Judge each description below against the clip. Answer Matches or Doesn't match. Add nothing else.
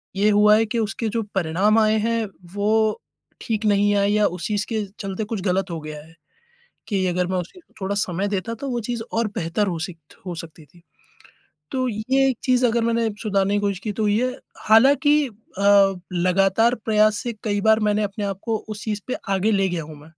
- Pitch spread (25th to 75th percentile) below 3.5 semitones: Matches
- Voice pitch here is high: Matches